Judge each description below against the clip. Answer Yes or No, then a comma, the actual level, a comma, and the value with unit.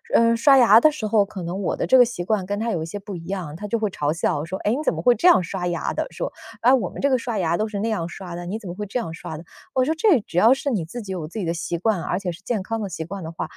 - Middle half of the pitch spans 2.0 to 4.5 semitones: No, average, 4.9 semitones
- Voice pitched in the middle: No, high, 200 Hz